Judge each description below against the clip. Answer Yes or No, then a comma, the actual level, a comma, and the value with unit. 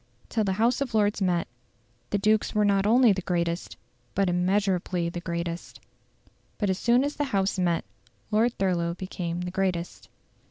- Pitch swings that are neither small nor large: Yes, average, 3.3 semitones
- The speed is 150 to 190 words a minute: Yes, average, 165 wpm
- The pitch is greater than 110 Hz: Yes, high, 190 Hz